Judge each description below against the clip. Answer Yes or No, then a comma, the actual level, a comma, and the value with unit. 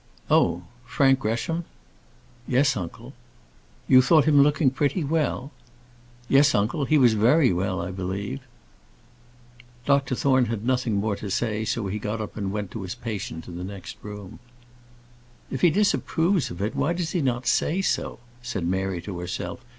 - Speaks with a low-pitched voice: Yes, low, 120 Hz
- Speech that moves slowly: No, average, 165 wpm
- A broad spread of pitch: Yes, wide, 5.8 semitones